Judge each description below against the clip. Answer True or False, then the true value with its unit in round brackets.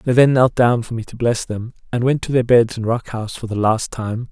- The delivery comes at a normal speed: False (290 wpm)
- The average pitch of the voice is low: True (120 Hz)